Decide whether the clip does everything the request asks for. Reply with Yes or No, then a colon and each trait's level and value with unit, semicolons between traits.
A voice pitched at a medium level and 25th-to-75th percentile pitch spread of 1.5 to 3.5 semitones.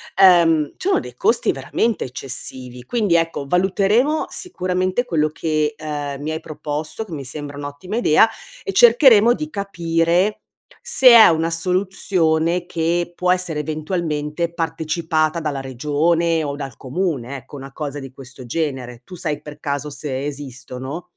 No: medium, 160 Hz; average, 4.0 semitones